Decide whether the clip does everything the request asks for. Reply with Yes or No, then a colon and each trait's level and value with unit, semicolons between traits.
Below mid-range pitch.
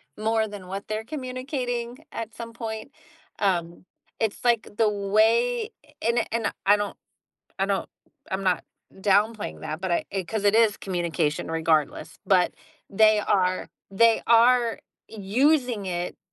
No: high, 215 Hz